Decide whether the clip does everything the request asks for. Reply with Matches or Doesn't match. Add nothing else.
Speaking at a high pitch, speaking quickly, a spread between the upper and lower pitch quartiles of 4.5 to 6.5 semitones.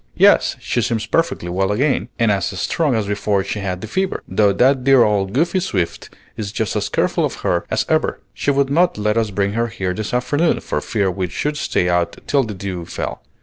Doesn't match